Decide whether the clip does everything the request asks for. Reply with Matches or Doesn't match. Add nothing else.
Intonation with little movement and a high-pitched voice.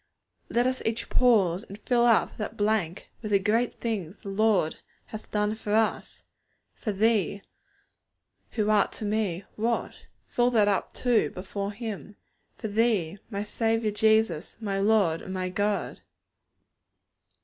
Matches